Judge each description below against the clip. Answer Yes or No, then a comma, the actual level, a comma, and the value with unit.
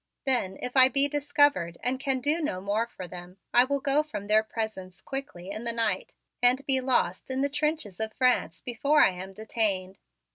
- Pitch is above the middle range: Yes, high, 240 Hz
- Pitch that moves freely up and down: Yes, wide, 5.9 semitones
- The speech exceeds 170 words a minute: Yes, average, 195 wpm